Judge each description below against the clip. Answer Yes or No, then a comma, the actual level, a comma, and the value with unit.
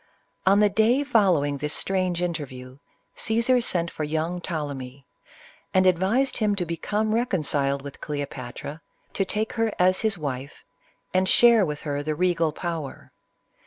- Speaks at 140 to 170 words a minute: Yes, average, 145 wpm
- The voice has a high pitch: No, medium, 175 Hz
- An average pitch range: No, wide, 6.0 semitones